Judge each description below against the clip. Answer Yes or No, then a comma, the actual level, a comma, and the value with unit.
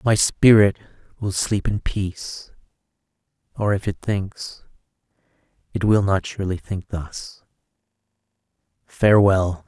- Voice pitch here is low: Yes, very low, 95 Hz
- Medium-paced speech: No, slow, 105 wpm